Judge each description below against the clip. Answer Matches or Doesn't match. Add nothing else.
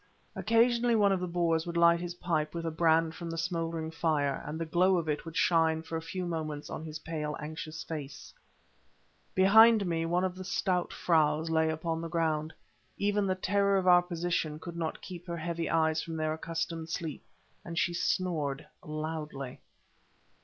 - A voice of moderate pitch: Matches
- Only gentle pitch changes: Matches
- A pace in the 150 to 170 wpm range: Doesn't match